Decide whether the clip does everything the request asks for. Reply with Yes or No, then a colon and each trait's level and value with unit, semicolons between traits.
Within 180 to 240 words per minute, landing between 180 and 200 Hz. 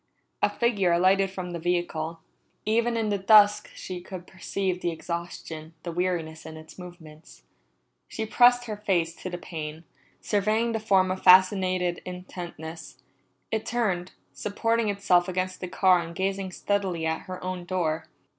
No: average, 155 wpm; medium, 185 Hz